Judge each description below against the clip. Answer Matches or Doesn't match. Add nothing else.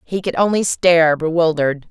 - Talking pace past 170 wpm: Doesn't match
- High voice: Doesn't match